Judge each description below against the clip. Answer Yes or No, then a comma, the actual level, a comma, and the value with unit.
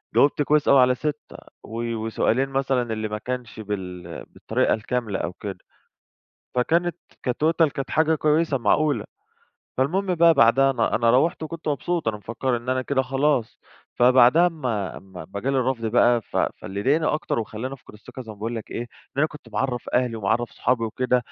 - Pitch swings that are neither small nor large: Yes, average, 4.3 semitones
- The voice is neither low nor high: No, low, 125 Hz